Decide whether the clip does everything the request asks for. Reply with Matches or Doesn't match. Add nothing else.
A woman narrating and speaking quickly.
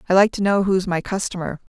Matches